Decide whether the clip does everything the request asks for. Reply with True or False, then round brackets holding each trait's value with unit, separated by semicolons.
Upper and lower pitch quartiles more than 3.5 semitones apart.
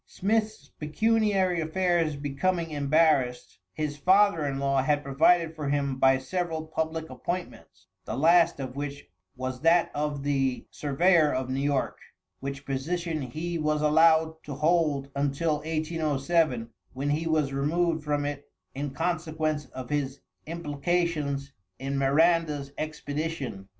False (3.1 semitones)